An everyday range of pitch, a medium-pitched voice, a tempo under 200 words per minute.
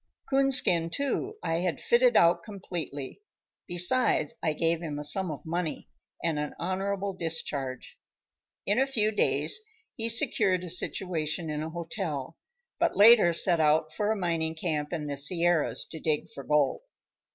Yes: average, 4.3 semitones; medium, 170 Hz; average, 155 wpm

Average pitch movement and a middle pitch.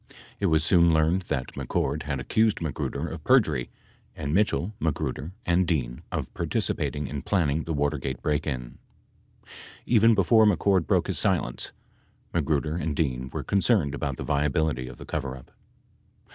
No: average, 4.0 semitones; very low, 75 Hz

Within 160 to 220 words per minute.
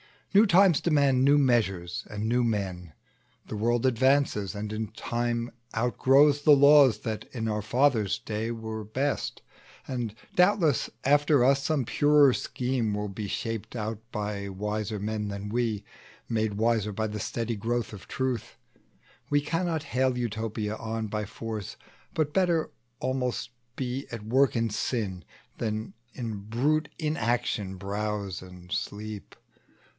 No: average, 140 wpm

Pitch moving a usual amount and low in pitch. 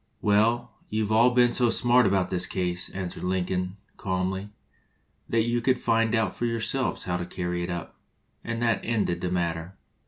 Yes: average, 4.2 semitones; low, 100 Hz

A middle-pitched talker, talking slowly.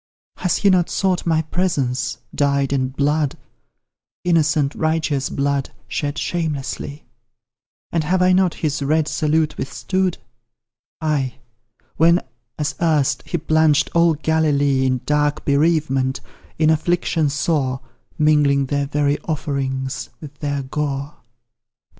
Yes: medium, 150 Hz; slow, 115 wpm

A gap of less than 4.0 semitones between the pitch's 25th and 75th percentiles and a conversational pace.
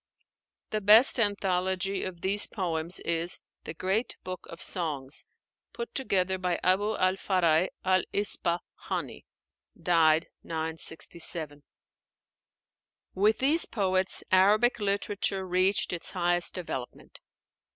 No: average, 2.9 semitones; slow, 110 wpm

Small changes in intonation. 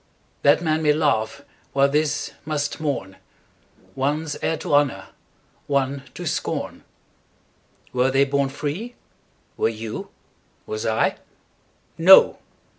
Yes: narrow, 2.3 semitones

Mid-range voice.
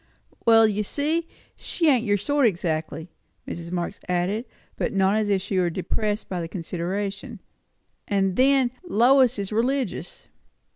No: high, 205 Hz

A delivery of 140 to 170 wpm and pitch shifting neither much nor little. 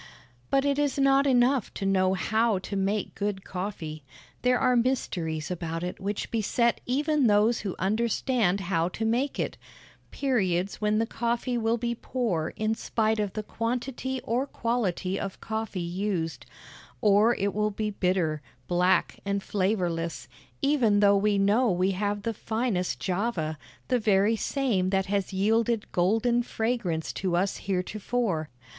Yes: average, 150 wpm; average, 4.0 semitones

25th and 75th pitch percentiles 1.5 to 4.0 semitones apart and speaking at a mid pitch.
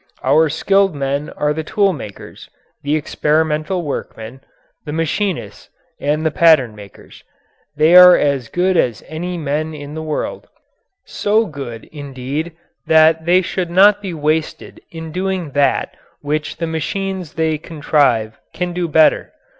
Yes: average, 3.3 semitones; medium, 155 Hz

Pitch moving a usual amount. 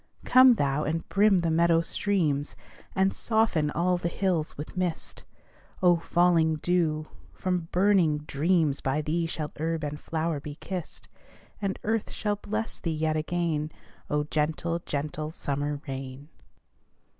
Yes: average, 3.2 semitones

